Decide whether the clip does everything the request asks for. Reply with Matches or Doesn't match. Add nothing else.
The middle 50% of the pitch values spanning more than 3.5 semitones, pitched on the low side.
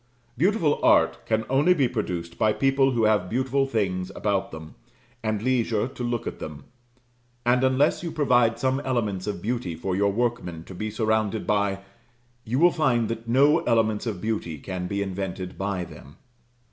Matches